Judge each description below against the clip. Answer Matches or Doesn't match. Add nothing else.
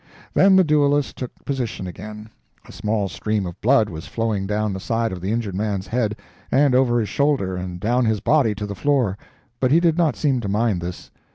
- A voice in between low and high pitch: Doesn't match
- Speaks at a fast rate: Matches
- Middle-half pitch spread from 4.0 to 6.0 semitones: Matches